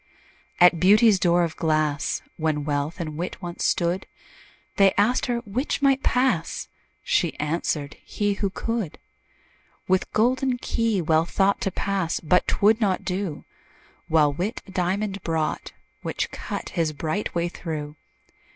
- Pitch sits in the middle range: Yes, medium, 180 Hz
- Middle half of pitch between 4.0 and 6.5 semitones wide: Yes, average, 4.5 semitones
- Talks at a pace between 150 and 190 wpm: No, average, 140 wpm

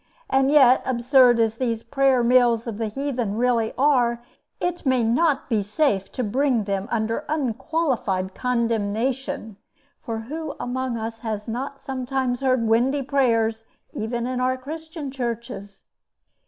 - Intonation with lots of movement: No, average, 3.0 semitones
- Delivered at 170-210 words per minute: No, average, 140 wpm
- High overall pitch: Yes, high, 245 Hz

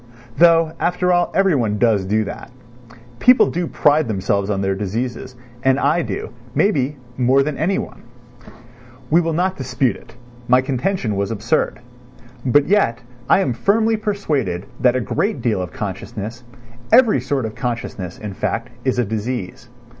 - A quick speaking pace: No, average, 155 wpm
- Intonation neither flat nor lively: No, wide, 7.4 semitones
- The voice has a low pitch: Yes, low, 125 Hz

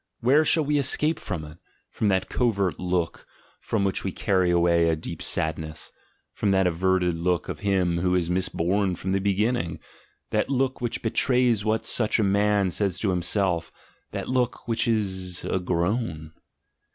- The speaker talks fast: No, average, 170 wpm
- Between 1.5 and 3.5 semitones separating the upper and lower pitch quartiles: No, average, 4.0 semitones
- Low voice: Yes, very low, 95 Hz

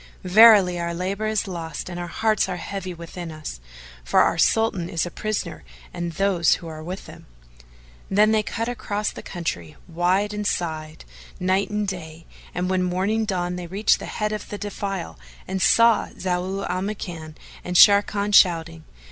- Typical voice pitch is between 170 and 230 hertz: Yes, medium, 185 Hz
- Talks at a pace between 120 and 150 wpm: No, average, 175 wpm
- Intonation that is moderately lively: Yes, average, 3.2 semitones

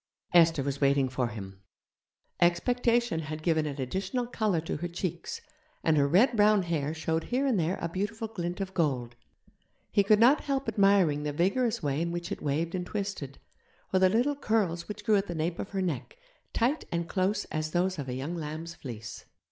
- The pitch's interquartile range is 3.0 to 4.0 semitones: No, average, 5.1 semitones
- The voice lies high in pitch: No, medium, 175 Hz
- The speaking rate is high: No, average, 195 wpm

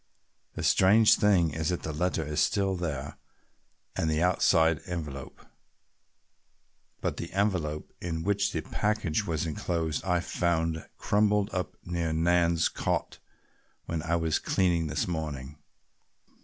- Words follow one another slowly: Yes, slow, 130 wpm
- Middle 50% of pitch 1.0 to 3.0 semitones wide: Yes, narrow, 2.6 semitones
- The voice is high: No, very low, 85 Hz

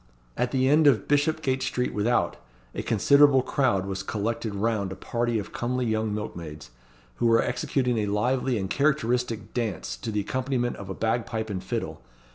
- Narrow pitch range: No, average, 3.8 semitones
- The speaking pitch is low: Yes, low, 115 Hz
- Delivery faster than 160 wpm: Yes, average, 170 wpm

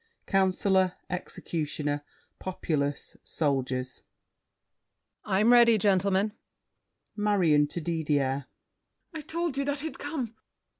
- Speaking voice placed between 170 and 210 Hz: Yes, medium, 185 Hz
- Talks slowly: Yes, slow, 95 wpm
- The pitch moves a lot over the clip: Yes, wide, 6.8 semitones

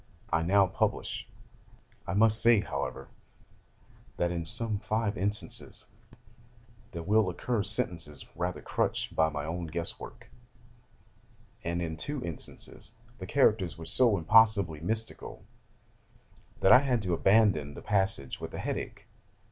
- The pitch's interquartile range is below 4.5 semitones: No, average, 4.8 semitones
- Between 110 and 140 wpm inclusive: Yes, slow, 135 wpm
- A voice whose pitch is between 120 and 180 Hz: No, very low, 95 Hz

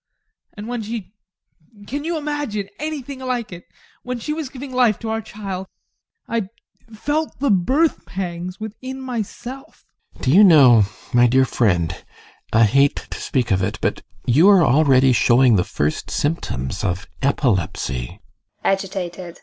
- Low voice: No, high, 190 Hz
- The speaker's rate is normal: Yes, average, 150 wpm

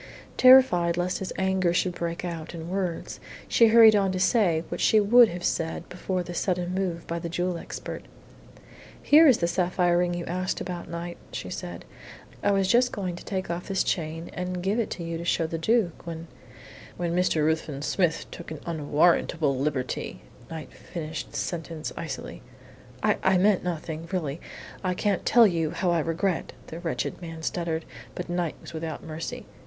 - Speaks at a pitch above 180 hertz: No, medium, 175 Hz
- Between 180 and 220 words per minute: Yes, average, 190 wpm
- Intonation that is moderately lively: No, narrow, 2.3 semitones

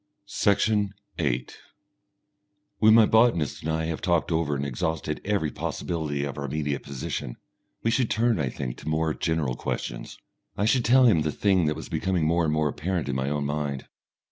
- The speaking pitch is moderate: No, very low, 80 Hz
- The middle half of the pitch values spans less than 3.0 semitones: No, average, 5.2 semitones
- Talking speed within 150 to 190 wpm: Yes, average, 185 wpm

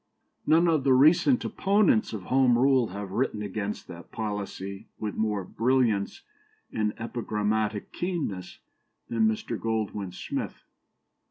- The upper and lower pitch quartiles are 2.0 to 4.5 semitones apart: Yes, average, 4.2 semitones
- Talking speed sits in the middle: No, slow, 120 wpm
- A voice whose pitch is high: No, low, 110 Hz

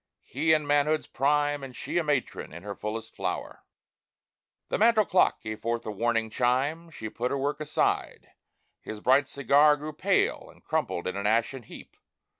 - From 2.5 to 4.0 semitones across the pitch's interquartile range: No, average, 4.6 semitones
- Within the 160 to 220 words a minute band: Yes, average, 175 wpm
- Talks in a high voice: No, low, 135 Hz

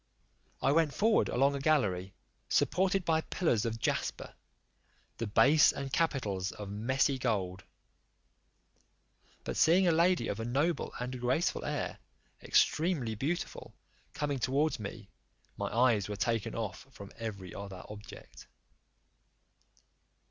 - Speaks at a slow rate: Yes, slow, 125 wpm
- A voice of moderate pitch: No, low, 125 Hz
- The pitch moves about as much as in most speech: No, wide, 6.7 semitones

